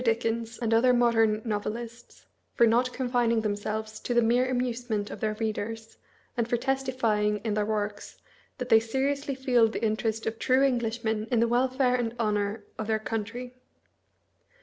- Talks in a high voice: Yes, high, 230 Hz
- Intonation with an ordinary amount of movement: No, narrow, 2.2 semitones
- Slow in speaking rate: No, average, 160 wpm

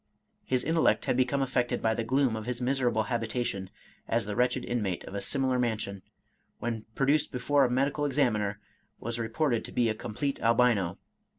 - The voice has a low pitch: Yes, low, 120 Hz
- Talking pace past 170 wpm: Yes, average, 180 wpm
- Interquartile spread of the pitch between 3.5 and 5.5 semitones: No, average, 3.1 semitones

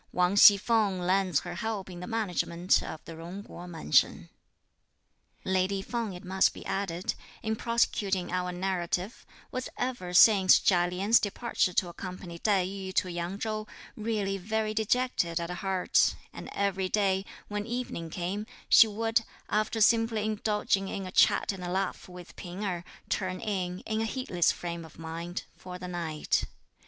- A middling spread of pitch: Yes, average, 3.2 semitones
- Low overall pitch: No, high, 190 Hz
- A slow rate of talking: No, average, 165 wpm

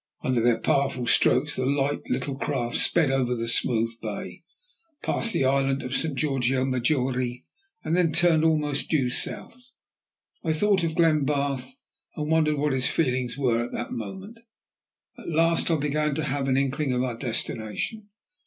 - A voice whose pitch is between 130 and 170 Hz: Yes, medium, 140 Hz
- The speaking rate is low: No, average, 165 wpm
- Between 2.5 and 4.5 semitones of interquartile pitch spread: Yes, average, 3.7 semitones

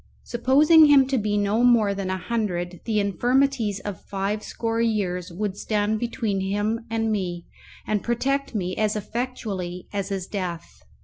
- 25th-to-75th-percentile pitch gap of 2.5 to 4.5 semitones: Yes, average, 3.4 semitones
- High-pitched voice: Yes, high, 210 Hz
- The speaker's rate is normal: Yes, average, 160 wpm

